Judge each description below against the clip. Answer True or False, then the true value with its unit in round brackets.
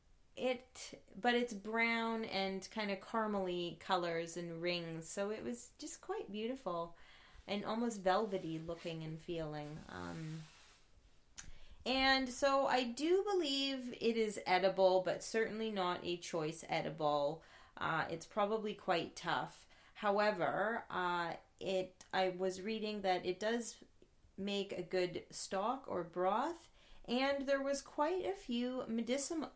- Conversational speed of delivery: False (130 wpm)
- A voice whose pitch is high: True (200 Hz)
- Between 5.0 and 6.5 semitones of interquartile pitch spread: True (5.4 semitones)